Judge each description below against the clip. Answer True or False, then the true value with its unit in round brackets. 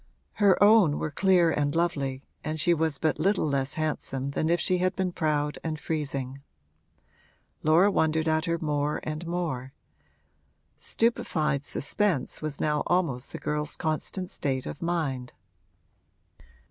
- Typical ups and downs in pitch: True (3.1 semitones)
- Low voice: False (155 Hz)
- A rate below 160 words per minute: True (140 wpm)